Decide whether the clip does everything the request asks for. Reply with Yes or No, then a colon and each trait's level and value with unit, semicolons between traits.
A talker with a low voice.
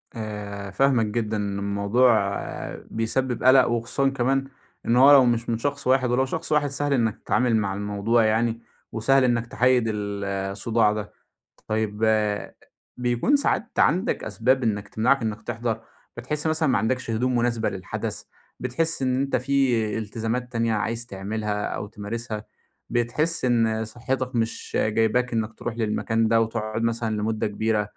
Yes: low, 115 Hz